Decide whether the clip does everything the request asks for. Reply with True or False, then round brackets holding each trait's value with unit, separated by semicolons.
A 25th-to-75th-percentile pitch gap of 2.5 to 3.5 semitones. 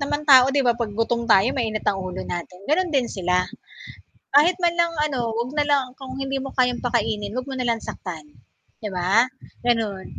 False (4.8 semitones)